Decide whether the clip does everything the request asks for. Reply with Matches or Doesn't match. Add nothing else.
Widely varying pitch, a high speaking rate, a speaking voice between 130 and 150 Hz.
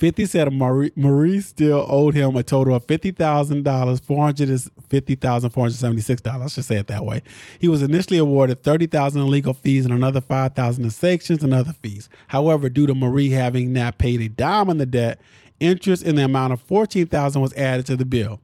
Doesn't match